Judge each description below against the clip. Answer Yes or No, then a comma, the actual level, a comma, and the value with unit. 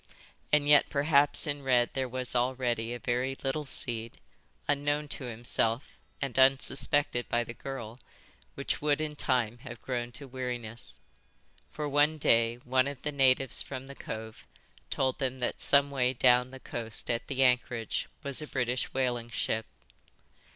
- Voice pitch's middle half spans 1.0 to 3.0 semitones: Yes, narrow, 2.6 semitones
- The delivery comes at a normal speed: Yes, average, 160 wpm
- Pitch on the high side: No, low, 130 Hz